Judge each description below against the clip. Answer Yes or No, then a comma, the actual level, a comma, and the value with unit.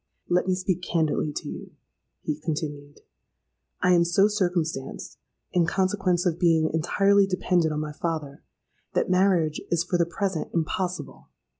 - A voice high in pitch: No, medium, 170 Hz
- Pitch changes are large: No, average, 2.7 semitones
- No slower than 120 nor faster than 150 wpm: Yes, average, 145 wpm